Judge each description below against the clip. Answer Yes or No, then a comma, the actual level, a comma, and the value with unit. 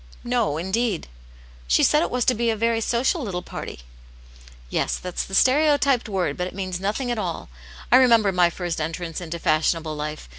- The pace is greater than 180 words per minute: Yes, average, 195 wpm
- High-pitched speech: Yes, high, 195 Hz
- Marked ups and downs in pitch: Yes, wide, 5.9 semitones